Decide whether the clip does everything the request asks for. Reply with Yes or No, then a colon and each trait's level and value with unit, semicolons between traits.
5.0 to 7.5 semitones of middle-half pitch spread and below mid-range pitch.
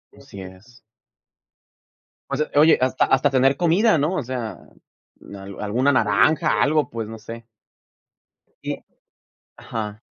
Yes: wide, 5.4 semitones; low, 125 Hz